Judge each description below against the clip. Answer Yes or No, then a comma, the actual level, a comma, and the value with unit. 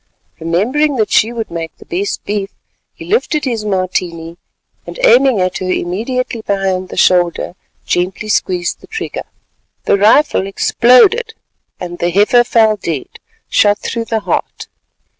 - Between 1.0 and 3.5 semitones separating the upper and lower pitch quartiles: No, average, 4.8 semitones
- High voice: Yes, high, 205 Hz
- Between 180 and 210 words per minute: No, average, 140 wpm